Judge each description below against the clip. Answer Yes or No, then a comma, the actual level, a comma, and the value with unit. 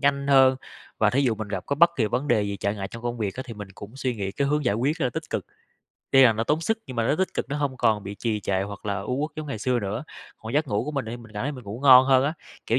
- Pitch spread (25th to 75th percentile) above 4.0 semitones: Yes, average, 4.7 semitones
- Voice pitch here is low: Yes, low, 120 Hz